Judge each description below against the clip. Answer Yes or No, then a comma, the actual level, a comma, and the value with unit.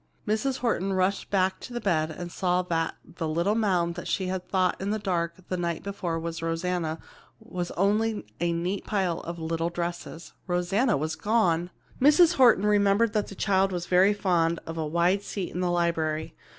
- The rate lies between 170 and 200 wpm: Yes, average, 185 wpm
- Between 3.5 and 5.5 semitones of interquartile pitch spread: No, average, 3.0 semitones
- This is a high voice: No, medium, 180 Hz